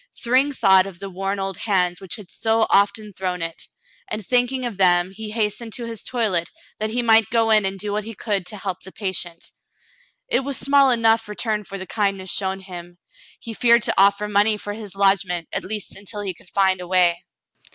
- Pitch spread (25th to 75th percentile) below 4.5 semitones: Yes, average, 2.9 semitones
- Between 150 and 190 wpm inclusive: No, fast, 205 wpm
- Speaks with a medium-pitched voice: No, high, 205 Hz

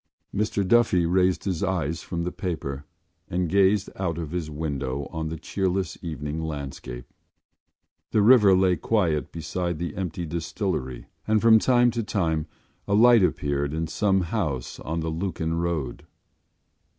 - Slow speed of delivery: No, average, 150 wpm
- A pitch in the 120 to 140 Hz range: No, very low, 85 Hz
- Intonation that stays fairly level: No, average, 3.8 semitones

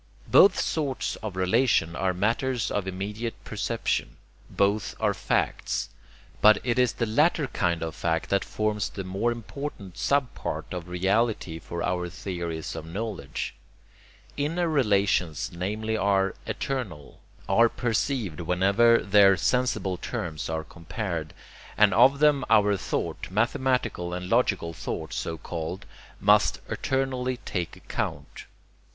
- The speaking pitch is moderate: No, low, 100 Hz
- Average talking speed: No, slow, 130 wpm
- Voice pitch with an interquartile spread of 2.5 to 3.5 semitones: No, average, 5.1 semitones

